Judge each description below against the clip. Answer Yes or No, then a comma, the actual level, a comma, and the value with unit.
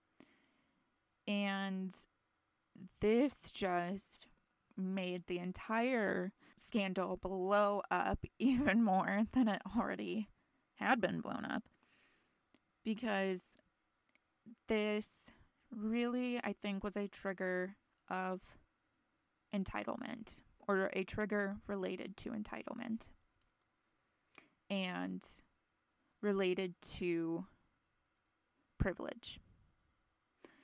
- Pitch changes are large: No, average, 2.8 semitones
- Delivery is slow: Yes, slow, 75 wpm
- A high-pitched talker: Yes, high, 200 Hz